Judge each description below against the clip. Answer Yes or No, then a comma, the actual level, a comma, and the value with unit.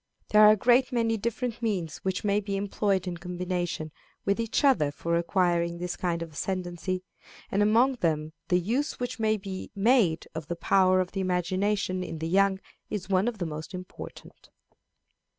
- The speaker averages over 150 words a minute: Yes, average, 180 wpm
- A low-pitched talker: No, high, 190 Hz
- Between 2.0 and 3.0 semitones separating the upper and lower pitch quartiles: No, average, 3.4 semitones